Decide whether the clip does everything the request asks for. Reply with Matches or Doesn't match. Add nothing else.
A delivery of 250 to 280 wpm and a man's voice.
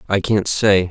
Doesn't match